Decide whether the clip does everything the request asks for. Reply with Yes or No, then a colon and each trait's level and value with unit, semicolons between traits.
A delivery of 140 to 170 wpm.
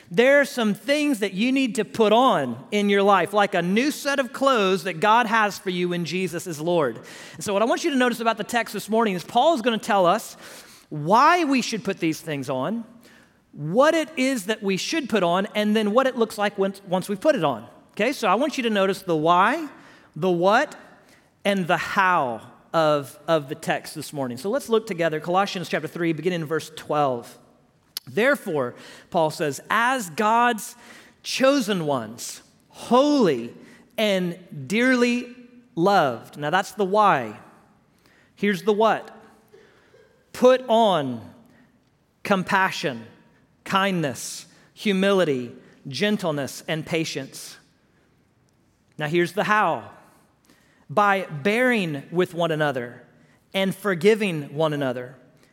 Yes: average, 155 wpm